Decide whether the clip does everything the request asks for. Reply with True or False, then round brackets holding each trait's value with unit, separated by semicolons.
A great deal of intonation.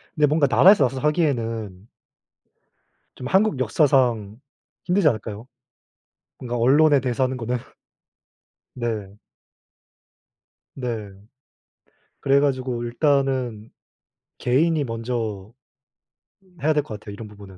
False (4.1 semitones)